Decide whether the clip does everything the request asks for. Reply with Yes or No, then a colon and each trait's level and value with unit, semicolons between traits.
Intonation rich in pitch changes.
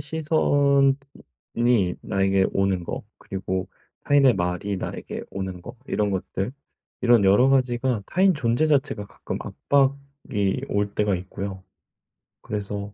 Yes: wide, 6.0 semitones